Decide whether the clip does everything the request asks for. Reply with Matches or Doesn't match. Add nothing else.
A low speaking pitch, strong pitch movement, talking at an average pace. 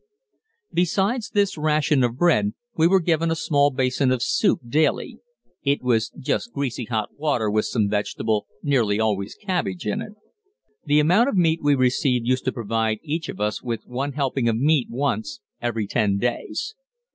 Matches